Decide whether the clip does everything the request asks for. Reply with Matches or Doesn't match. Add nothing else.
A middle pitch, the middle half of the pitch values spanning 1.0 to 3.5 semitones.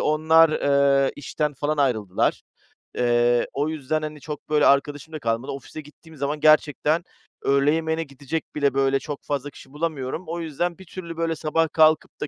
Matches